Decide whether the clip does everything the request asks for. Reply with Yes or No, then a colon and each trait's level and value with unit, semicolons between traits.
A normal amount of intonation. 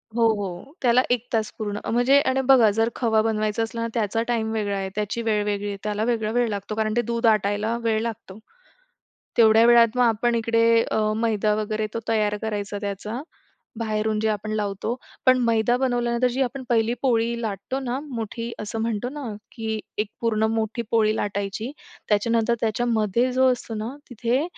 No: narrow, 1.9 semitones